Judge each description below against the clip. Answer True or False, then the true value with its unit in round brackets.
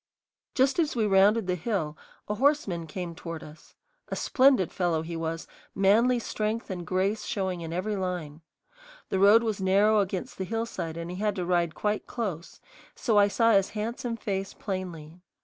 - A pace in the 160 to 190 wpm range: True (175 wpm)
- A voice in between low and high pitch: False (195 Hz)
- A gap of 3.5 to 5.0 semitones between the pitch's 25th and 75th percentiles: True (3.9 semitones)